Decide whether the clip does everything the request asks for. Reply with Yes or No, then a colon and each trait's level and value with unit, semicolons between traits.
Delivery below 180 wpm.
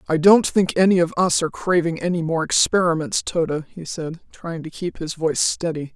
No: average, 200 wpm